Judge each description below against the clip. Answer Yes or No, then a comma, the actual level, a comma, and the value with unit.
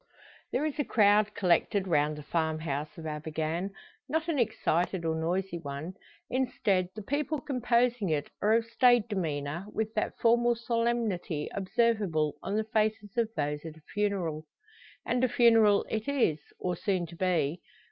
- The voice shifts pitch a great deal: Yes, wide, 6.3 semitones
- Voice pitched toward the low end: No, high, 200 Hz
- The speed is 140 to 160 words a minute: Yes, average, 155 wpm